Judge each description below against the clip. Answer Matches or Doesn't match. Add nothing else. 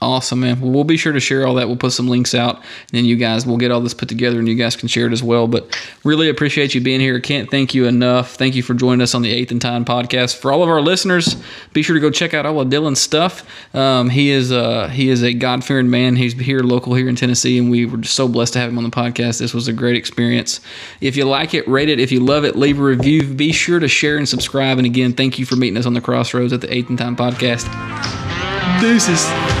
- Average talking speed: Doesn't match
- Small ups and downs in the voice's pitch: Matches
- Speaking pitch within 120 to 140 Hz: Matches